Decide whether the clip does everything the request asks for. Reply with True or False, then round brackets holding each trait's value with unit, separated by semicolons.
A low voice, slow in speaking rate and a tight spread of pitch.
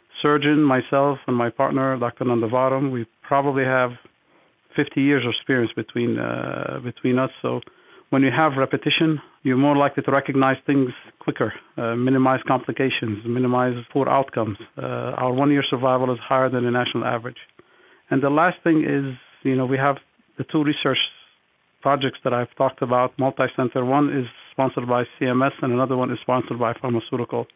False (130 Hz; 165 wpm; 2.0 semitones)